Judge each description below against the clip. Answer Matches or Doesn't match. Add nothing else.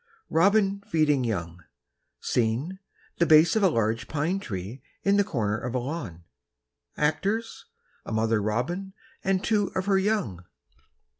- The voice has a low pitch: Doesn't match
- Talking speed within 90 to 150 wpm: Matches